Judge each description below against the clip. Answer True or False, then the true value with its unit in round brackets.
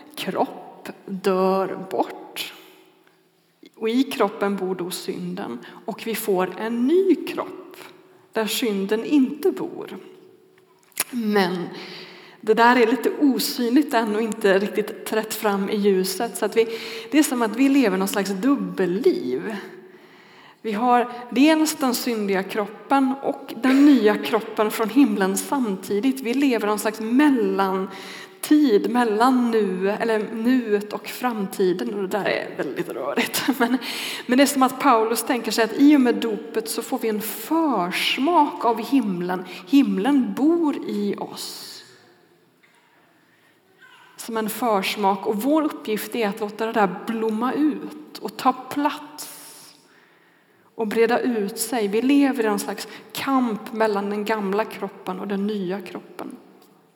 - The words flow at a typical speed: True (140 wpm)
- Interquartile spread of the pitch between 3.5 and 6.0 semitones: True (4.9 semitones)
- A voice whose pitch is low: False (225 Hz)